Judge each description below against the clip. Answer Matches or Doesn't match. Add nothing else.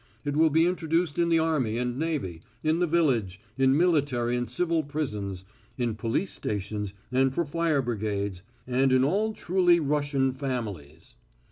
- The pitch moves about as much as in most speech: Doesn't match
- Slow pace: Doesn't match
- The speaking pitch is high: Doesn't match